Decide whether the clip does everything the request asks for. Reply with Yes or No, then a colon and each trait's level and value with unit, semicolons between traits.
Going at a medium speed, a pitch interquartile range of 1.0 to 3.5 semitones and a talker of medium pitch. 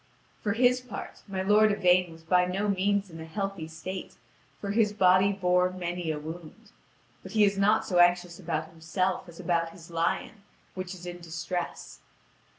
Yes: average, 175 wpm; average, 2.7 semitones; medium, 180 Hz